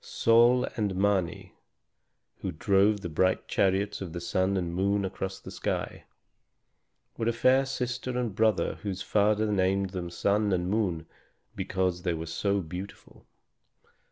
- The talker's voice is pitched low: Yes, low, 100 Hz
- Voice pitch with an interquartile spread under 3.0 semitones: Yes, narrow, 2.6 semitones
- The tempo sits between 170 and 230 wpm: No, average, 145 wpm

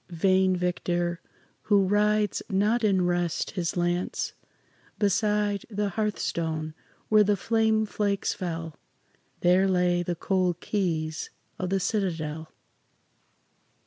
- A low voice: No, medium, 185 Hz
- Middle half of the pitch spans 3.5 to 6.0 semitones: No, average, 3.0 semitones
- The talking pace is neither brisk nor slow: No, slow, 110 wpm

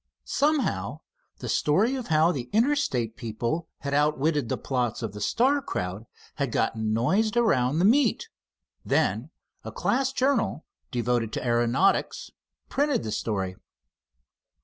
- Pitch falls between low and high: Yes, medium, 145 Hz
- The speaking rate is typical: No, slow, 130 wpm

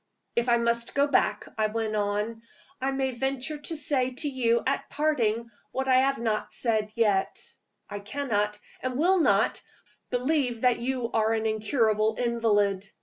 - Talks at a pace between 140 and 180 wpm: Yes, average, 160 wpm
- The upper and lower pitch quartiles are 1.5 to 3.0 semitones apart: No, average, 3.6 semitones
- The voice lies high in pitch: Yes, high, 235 Hz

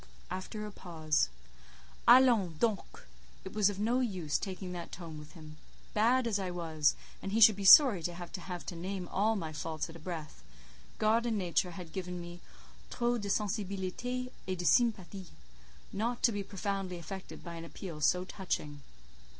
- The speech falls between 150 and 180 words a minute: Yes, average, 165 wpm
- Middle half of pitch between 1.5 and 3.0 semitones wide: No, average, 3.7 semitones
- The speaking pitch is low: No, high, 190 Hz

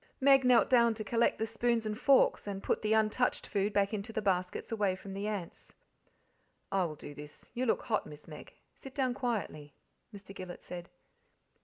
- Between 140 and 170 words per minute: No, average, 190 wpm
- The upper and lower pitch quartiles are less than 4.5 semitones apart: Yes, average, 3.6 semitones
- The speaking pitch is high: Yes, high, 210 Hz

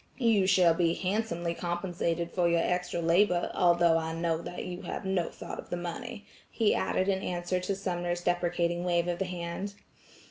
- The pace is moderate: Yes, average, 180 wpm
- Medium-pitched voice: Yes, medium, 175 Hz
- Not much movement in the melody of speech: Yes, narrow, 1.5 semitones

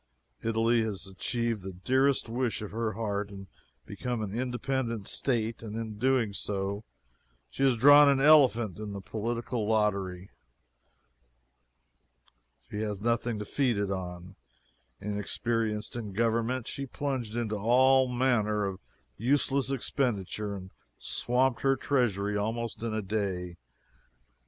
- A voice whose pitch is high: No, low, 110 Hz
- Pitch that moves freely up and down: No, average, 3.3 semitones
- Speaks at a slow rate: Yes, slow, 130 wpm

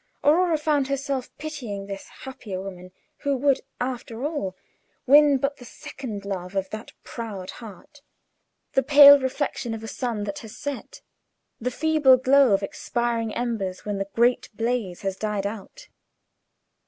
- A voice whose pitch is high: Yes, high, 240 Hz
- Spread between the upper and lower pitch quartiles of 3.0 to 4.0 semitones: No, wide, 5.5 semitones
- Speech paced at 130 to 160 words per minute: Yes, average, 150 wpm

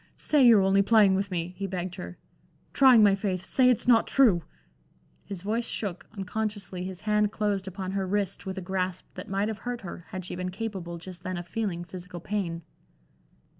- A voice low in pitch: No, high, 195 Hz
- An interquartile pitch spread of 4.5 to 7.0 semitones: No, narrow, 2.5 semitones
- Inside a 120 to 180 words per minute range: No, average, 195 wpm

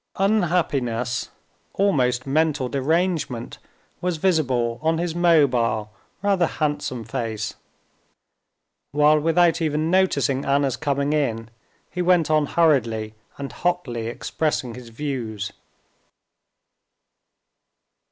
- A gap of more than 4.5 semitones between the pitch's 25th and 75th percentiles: Yes, average, 5.2 semitones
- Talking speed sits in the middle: No, slow, 95 wpm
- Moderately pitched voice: Yes, medium, 145 Hz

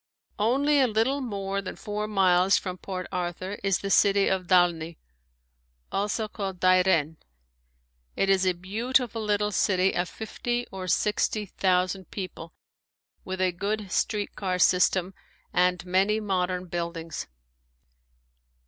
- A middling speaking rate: No, slow, 130 wpm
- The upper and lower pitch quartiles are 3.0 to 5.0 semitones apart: No, narrow, 2.5 semitones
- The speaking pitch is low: No, high, 190 Hz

